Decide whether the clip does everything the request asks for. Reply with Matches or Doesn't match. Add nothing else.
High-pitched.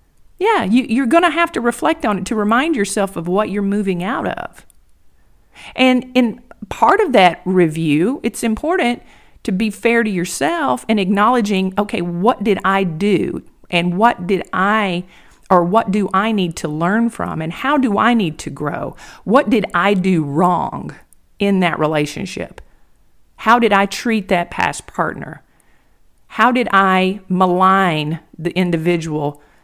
Matches